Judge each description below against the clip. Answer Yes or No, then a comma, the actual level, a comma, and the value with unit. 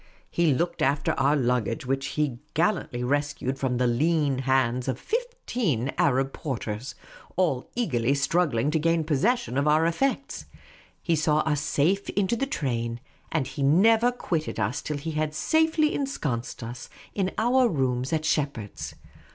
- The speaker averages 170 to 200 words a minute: No, average, 150 wpm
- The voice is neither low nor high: Yes, medium, 150 Hz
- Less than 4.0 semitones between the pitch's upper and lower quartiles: No, average, 4.9 semitones